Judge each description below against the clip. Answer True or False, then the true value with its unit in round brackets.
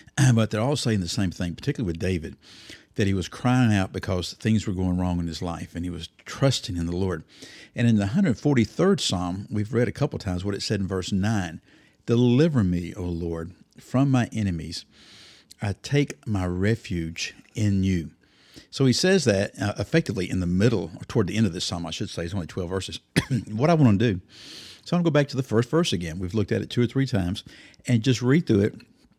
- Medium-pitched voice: False (105 Hz)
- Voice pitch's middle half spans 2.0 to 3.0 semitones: False (5.3 semitones)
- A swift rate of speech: True (225 wpm)